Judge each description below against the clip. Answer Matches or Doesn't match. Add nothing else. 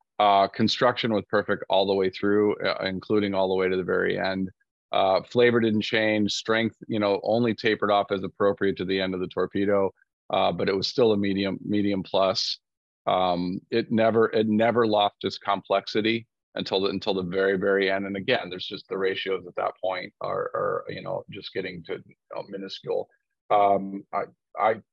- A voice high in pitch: Doesn't match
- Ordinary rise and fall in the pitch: Doesn't match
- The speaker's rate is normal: Matches